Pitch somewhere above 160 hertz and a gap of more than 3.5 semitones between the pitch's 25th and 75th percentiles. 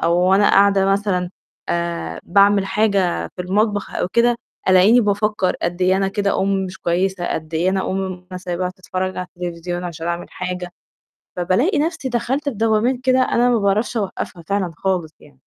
No: high, 190 Hz; average, 2.7 semitones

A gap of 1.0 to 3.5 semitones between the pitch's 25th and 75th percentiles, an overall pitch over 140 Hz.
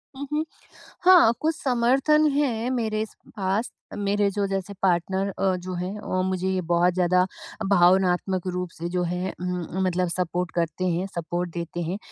Yes: average, 2.8 semitones; medium, 185 Hz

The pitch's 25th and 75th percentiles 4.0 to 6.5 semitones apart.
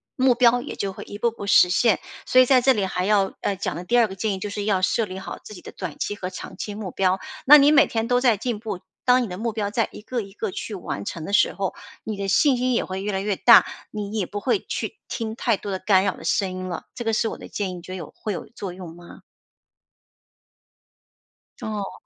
No: average, 3.6 semitones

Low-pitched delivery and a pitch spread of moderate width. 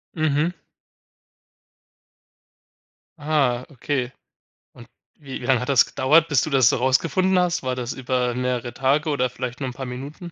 Yes: low, 130 Hz; average, 3.2 semitones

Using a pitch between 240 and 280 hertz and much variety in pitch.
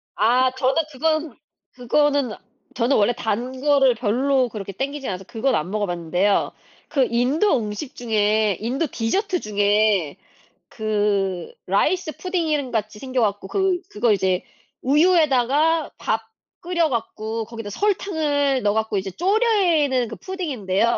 Yes: high, 245 Hz; wide, 5.9 semitones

